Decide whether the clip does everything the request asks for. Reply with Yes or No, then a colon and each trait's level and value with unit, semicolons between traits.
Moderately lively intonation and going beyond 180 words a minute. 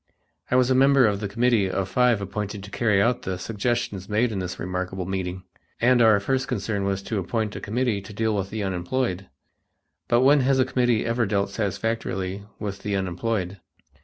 Yes: average, 3.7 semitones; average, 190 wpm